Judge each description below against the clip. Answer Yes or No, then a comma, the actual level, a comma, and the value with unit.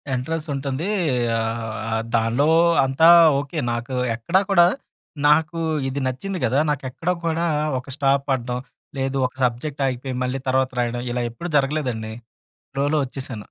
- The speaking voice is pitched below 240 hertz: Yes, low, 135 Hz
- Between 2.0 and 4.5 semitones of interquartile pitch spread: Yes, average, 3.5 semitones